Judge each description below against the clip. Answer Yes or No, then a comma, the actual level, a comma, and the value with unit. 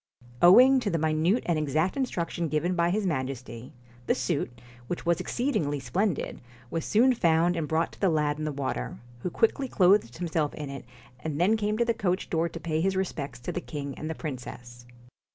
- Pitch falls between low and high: Yes, medium, 165 Hz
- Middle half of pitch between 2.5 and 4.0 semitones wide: No, average, 4.5 semitones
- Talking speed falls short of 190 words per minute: No, fast, 205 wpm